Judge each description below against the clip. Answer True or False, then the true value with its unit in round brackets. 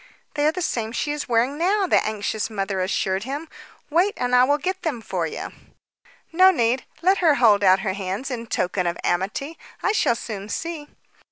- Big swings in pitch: True (8.0 semitones)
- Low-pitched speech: False (245 Hz)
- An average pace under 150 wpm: False (195 wpm)